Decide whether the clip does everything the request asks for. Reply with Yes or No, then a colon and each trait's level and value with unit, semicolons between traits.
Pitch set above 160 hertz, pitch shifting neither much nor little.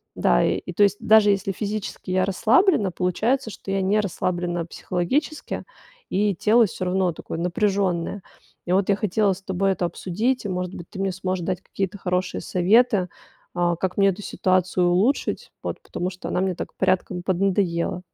No: high, 190 Hz; narrow, 2.3 semitones